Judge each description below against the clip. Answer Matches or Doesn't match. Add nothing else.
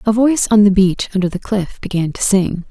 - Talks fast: Matches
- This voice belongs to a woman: Matches